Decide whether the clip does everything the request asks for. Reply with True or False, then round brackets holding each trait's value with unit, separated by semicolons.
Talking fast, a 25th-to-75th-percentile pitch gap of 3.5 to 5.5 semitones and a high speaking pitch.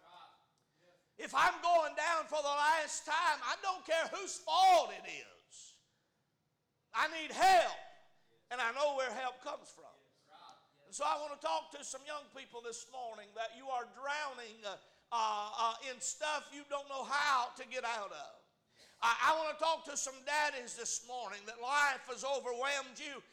False (175 wpm; 3.9 semitones; 280 Hz)